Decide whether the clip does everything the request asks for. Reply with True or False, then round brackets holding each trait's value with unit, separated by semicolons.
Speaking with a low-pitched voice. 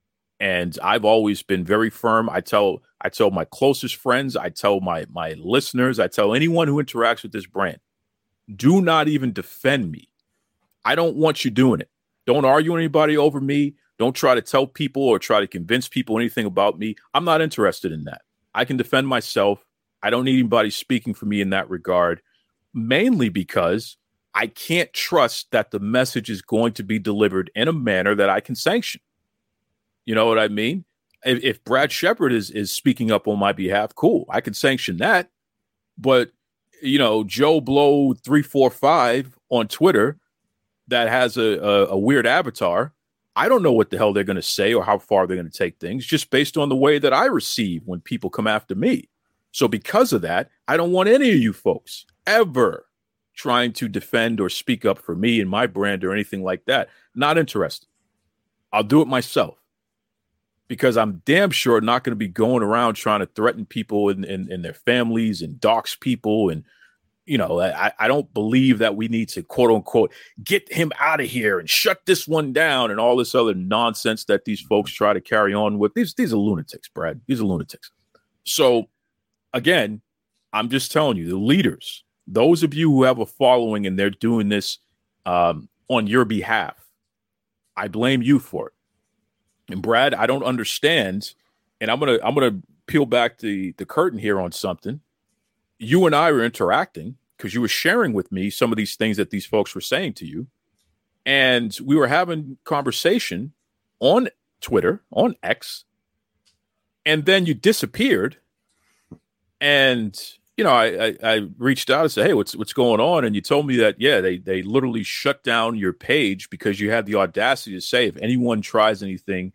True (115 Hz)